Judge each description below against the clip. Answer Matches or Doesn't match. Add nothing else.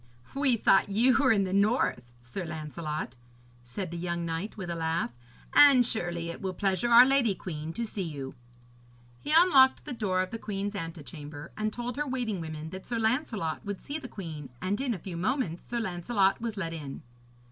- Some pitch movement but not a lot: Doesn't match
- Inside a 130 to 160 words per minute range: Doesn't match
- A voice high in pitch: Matches